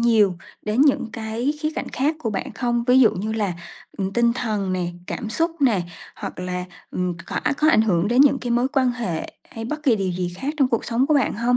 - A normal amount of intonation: Yes, average, 4.6 semitones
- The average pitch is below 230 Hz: No, high, 235 Hz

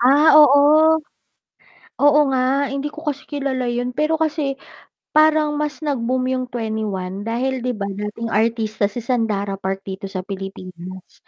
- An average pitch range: No, wide, 5.7 semitones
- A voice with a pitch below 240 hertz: No, very high, 250 Hz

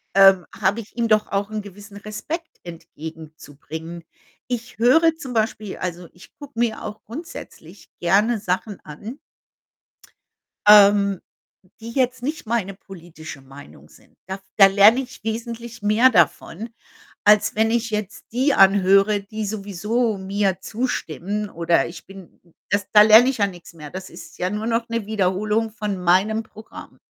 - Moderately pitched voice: No, high, 210 Hz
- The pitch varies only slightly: No, average, 3.3 semitones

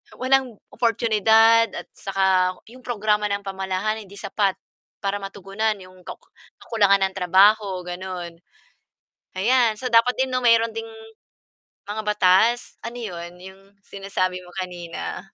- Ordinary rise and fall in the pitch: Yes, average, 3.2 semitones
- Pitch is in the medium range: No, high, 200 Hz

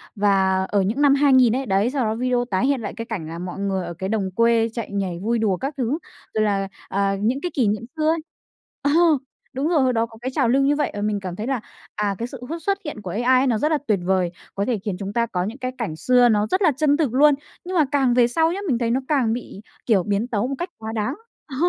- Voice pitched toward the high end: Yes, high, 235 Hz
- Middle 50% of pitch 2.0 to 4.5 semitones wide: No, average, 5.1 semitones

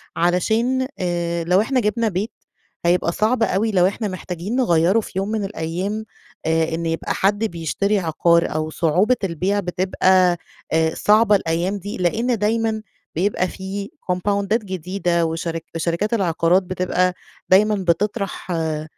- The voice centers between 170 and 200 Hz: Yes, medium, 185 Hz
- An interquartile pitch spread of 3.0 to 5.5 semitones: Yes, average, 3.6 semitones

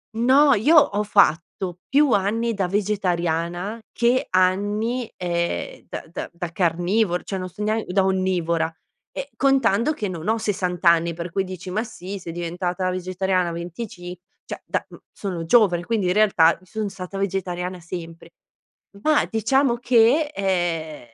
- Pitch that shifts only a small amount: No, average, 3.9 semitones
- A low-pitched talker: No, high, 190 Hz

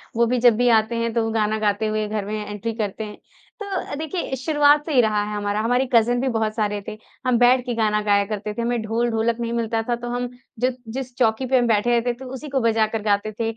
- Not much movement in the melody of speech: Yes, narrow, 2.3 semitones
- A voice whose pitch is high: Yes, high, 230 Hz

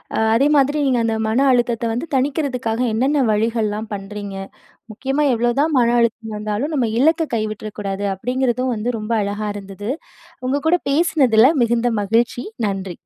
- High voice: Yes, high, 235 Hz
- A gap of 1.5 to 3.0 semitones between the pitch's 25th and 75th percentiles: No, average, 3.7 semitones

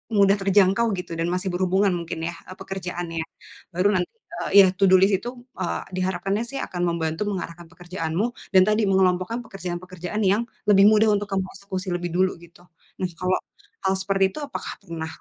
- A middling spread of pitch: No, narrow, 2.0 semitones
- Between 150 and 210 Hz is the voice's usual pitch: Yes, medium, 185 Hz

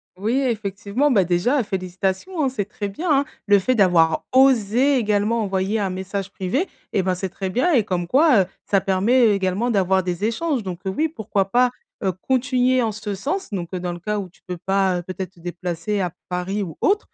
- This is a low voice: No, high, 200 Hz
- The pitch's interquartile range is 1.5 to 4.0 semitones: No, average, 4.8 semitones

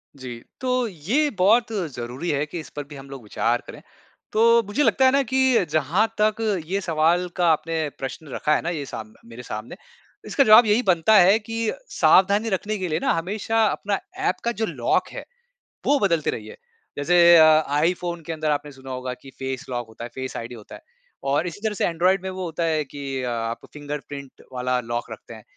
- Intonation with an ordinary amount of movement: No, wide, 7.1 semitones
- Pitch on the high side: No, medium, 160 Hz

